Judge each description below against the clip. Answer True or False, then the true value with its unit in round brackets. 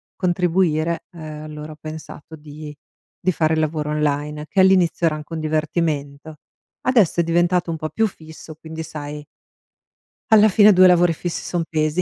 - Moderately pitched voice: True (160 Hz)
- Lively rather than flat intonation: False (2.4 semitones)